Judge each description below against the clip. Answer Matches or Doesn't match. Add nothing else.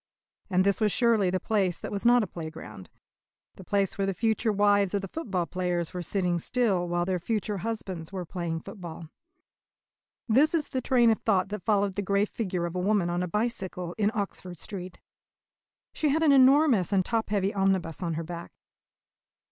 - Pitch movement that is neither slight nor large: Matches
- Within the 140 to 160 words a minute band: Doesn't match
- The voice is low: Doesn't match